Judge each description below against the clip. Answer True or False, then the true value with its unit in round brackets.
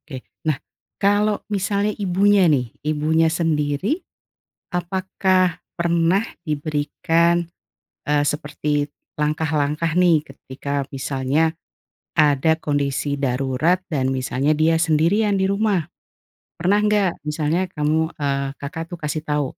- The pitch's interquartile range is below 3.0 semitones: False (3.6 semitones)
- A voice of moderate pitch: True (160 Hz)